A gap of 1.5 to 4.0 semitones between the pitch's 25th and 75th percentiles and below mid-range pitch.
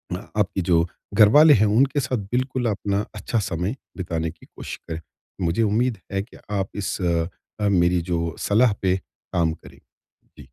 No: average, 5.2 semitones; low, 100 Hz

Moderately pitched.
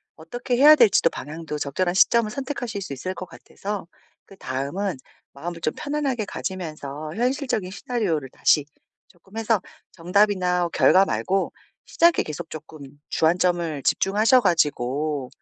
Yes: medium, 180 Hz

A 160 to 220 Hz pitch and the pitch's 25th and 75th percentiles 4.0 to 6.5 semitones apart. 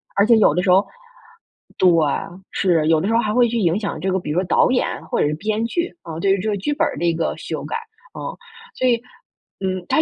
Yes: high, 195 Hz; average, 4.5 semitones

